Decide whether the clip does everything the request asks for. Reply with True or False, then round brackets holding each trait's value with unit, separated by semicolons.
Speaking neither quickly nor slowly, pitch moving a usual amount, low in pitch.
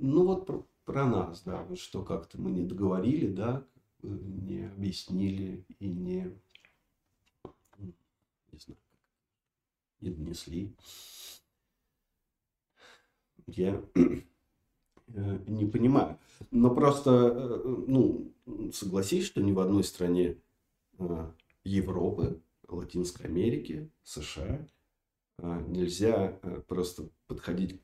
False (85 wpm; 3.9 semitones; 95 Hz)